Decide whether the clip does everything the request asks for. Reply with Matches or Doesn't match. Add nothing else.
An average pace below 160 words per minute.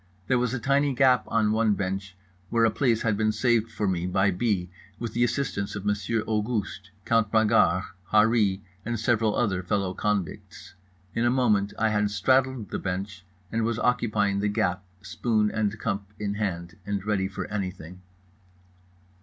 Doesn't match